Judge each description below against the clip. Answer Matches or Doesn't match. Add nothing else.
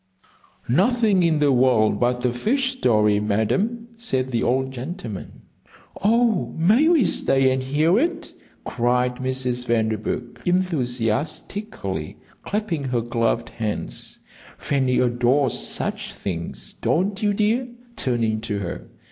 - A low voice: Matches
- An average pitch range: Doesn't match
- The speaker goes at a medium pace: Doesn't match